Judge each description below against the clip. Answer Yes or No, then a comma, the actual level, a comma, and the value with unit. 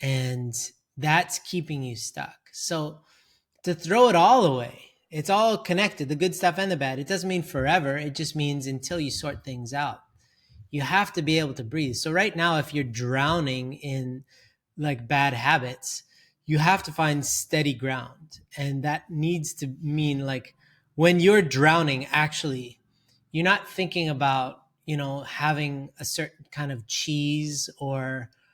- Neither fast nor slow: Yes, average, 165 wpm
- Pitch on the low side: No, medium, 150 Hz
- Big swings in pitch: No, average, 3.3 semitones